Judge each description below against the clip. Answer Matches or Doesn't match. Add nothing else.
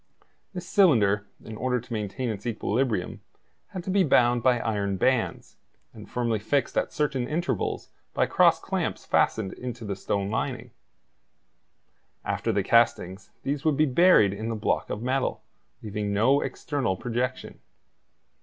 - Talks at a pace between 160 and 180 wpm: Doesn't match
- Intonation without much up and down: Doesn't match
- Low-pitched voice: Matches